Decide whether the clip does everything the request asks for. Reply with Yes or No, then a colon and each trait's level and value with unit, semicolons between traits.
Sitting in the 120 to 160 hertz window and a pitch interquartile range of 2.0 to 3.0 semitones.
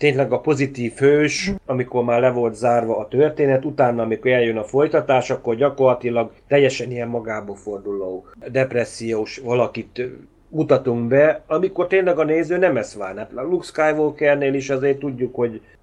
No: low, 130 Hz; average, 3.8 semitones